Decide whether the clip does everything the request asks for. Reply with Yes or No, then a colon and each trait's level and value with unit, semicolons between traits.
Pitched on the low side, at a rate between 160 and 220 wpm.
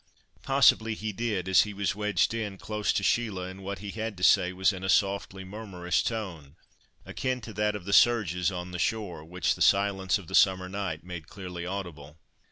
Yes: very low, 95 Hz; average, 200 wpm